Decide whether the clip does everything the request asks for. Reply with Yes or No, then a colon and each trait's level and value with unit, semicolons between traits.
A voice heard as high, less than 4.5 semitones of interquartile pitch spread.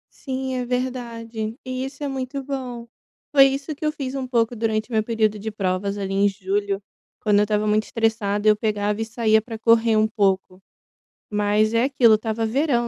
Yes: high, 225 Hz; average, 3.3 semitones